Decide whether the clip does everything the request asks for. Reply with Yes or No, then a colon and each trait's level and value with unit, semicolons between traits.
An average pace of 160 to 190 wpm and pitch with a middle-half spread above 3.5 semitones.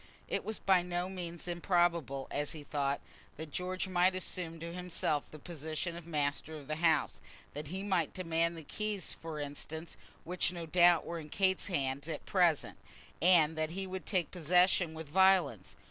No: average, 175 wpm; average, 2.8 semitones